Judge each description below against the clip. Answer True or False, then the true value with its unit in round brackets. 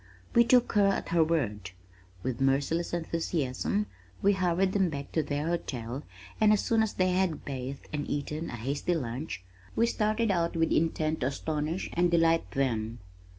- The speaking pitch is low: False (165 Hz)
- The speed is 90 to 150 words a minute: False (165 wpm)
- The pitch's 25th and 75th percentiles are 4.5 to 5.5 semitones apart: True (5.1 semitones)